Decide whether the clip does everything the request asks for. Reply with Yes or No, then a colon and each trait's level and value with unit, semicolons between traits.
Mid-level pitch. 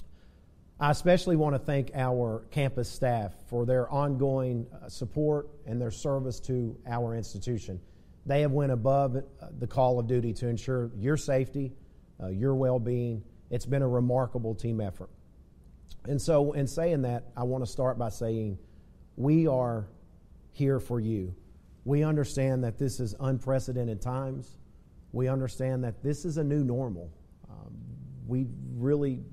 No: low, 125 Hz